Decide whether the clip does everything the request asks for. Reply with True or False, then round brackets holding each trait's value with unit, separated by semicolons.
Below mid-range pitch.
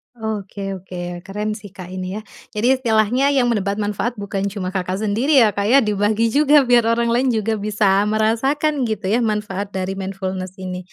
False (210 Hz)